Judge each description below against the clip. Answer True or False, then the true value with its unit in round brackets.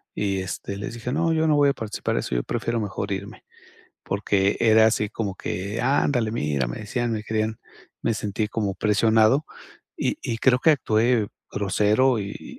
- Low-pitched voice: True (110 Hz)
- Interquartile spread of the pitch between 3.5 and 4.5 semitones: False (2.9 semitones)